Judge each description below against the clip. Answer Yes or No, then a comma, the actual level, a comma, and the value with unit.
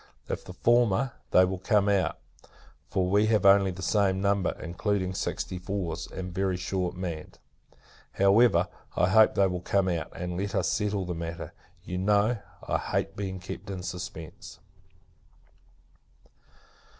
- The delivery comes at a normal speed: Yes, average, 150 wpm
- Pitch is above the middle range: No, very low, 95 Hz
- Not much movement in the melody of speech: Yes, narrow, 2.0 semitones